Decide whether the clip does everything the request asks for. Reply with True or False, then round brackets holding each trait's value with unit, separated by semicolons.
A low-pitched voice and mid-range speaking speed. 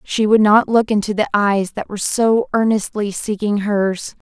False (210 Hz; 180 wpm)